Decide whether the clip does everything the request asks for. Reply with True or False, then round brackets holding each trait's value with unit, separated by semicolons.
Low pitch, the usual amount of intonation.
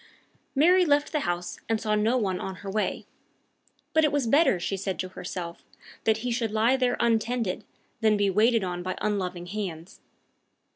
False (215 Hz; 4.8 semitones)